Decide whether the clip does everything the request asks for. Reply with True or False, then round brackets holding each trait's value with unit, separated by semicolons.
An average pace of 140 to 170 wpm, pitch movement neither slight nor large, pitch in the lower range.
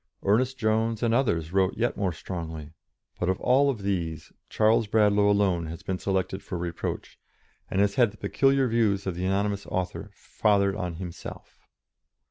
True (165 wpm; 3.3 semitones; 100 Hz)